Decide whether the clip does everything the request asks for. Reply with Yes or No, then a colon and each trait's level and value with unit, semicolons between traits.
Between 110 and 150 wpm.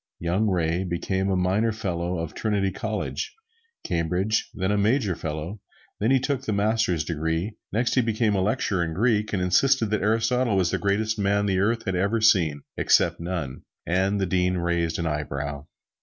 No: average, 175 wpm